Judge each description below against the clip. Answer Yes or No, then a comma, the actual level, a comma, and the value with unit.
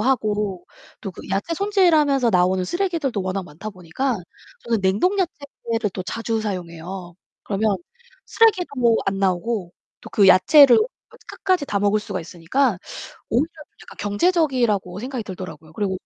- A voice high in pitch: Yes, high, 210 Hz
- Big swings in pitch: Yes, wide, 6.3 semitones